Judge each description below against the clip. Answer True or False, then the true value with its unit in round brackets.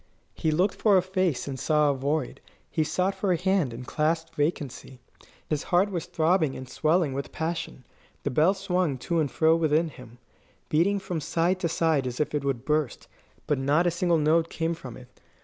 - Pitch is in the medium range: True (160 Hz)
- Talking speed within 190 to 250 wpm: True (200 wpm)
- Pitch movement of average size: True (3.7 semitones)